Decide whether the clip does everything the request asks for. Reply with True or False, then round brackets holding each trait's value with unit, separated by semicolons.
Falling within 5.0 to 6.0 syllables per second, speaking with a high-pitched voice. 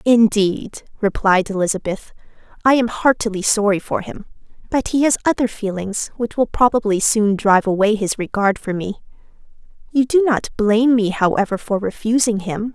True (5.1 syllables/s; 215 Hz)